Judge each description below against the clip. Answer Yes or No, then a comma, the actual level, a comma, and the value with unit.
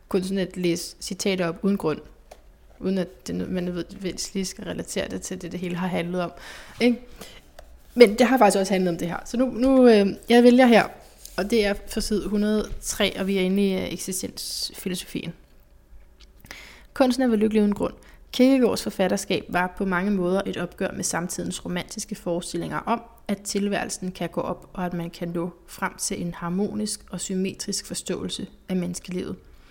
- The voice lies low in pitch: No, high, 190 Hz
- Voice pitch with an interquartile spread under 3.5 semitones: Yes, average, 2.8 semitones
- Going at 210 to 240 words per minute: No, average, 180 wpm